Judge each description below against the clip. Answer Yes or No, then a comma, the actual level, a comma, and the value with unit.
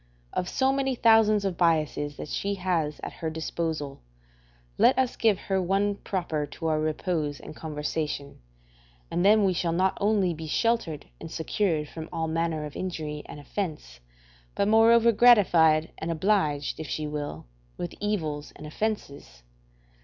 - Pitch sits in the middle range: Yes, medium, 165 Hz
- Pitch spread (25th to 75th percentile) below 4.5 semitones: No, average, 4.9 semitones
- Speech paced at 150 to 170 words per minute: Yes, average, 155 wpm